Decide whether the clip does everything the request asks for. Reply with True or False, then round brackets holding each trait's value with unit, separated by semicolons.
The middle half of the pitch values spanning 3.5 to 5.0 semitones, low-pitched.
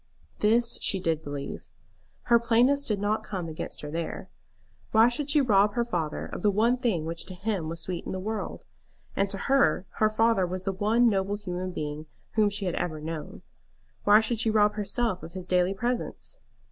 False (4.2 semitones; 205 Hz)